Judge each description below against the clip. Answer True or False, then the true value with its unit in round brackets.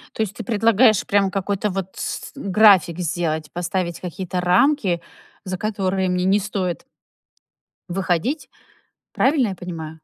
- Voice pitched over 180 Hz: True (190 Hz)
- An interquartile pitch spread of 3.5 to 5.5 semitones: False (2.8 semitones)